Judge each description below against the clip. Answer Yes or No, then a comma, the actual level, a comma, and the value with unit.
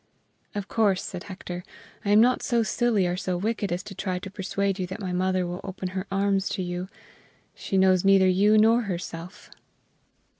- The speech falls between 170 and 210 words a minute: Yes, average, 190 wpm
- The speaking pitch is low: No, high, 190 Hz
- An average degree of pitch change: No, narrow, 2.1 semitones